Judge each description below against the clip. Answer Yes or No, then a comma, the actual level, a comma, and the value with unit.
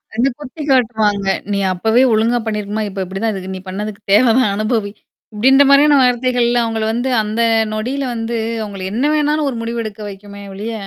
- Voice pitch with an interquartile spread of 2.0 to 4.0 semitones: Yes, average, 3.3 semitones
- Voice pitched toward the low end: No, high, 225 Hz